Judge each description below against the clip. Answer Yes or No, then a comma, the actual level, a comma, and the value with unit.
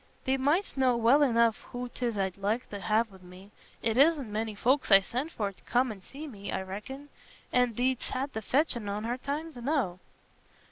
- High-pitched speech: Yes, high, 235 Hz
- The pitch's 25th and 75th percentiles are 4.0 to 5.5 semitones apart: Yes, average, 4.4 semitones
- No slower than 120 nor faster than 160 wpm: No, average, 200 wpm